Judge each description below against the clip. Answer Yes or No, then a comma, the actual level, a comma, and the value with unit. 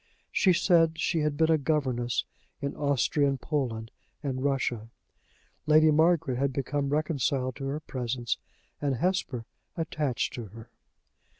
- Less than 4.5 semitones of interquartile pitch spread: Yes, average, 3.5 semitones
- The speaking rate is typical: No, slow, 130 wpm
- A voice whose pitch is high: No, medium, 140 Hz